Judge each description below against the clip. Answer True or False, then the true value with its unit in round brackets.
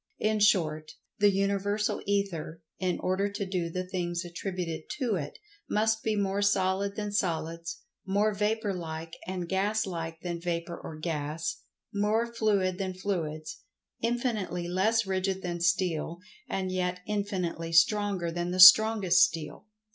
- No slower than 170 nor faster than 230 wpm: False (140 wpm)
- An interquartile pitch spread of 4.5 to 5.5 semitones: False (3.1 semitones)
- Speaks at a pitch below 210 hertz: True (185 Hz)